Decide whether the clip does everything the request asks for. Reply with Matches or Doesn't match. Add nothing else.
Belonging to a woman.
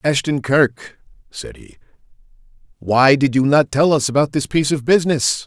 Doesn't match